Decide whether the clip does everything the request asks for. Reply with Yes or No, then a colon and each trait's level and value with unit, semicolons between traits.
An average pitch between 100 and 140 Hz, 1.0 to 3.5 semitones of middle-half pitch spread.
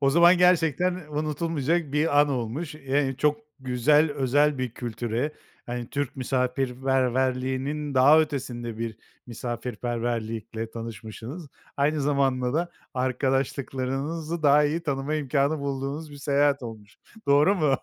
Yes: low, 135 Hz; average, 3.1 semitones